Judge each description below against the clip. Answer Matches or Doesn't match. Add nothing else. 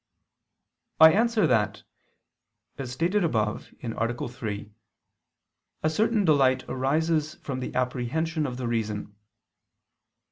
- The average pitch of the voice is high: Doesn't match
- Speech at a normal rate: Doesn't match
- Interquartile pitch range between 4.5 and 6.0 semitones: Matches